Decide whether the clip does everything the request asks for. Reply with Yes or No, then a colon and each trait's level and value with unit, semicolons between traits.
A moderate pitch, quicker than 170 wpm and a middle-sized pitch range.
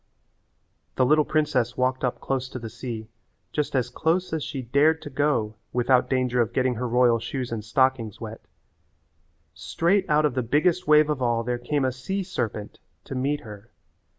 No: low, 130 Hz; average, 180 wpm; average, 3.8 semitones